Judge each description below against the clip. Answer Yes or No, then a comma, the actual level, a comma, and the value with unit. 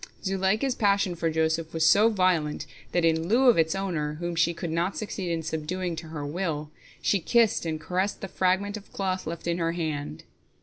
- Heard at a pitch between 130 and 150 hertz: No, medium, 170 Hz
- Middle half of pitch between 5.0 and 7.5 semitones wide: No, average, 3.1 semitones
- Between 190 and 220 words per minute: Yes, average, 200 wpm